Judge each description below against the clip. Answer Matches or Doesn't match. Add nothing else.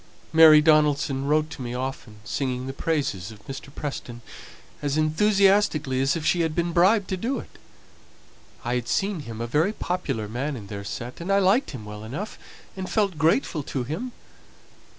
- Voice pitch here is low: Doesn't match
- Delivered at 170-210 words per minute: Matches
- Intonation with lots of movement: Matches